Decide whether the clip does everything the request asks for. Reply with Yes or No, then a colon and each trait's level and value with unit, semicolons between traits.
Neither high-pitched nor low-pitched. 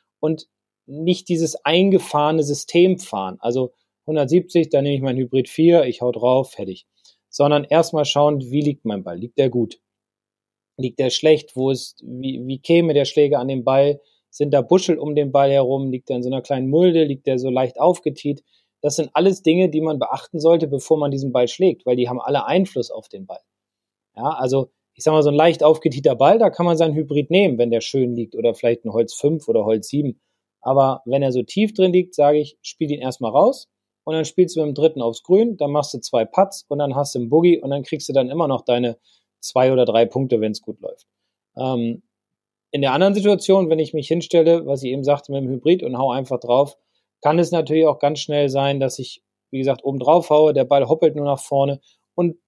Yes: medium, 145 Hz